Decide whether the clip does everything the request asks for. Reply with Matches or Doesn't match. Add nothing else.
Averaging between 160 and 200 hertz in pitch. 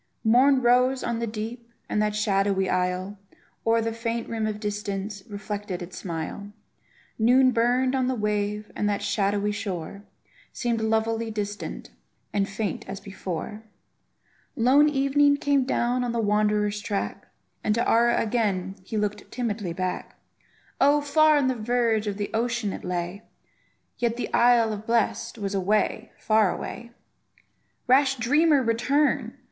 Doesn't match